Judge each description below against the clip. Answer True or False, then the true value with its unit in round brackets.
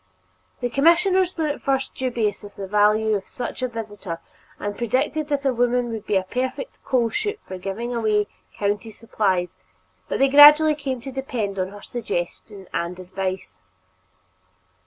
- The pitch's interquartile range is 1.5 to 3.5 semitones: False (5.1 semitones)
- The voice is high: True (230 Hz)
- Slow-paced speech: False (160 wpm)